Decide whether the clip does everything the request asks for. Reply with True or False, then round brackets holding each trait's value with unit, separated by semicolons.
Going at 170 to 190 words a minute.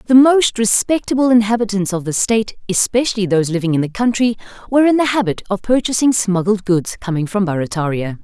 True (175 wpm)